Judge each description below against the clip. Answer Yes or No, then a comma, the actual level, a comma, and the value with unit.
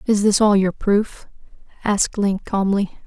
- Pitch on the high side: Yes, high, 200 Hz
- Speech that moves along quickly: No, average, 155 wpm